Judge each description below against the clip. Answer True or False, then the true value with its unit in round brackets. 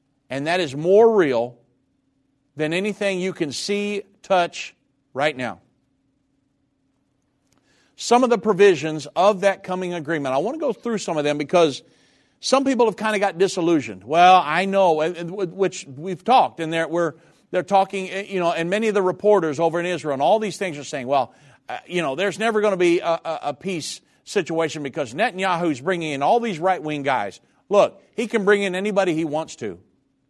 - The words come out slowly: False (185 wpm)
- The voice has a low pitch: False (175 Hz)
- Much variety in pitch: False (4.9 semitones)